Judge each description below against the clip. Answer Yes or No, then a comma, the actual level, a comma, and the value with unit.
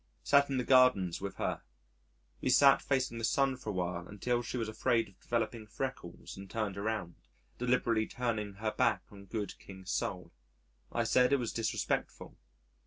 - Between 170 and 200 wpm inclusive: Yes, average, 175 wpm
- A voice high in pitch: No, low, 115 Hz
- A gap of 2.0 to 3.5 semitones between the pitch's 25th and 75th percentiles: No, average, 4.1 semitones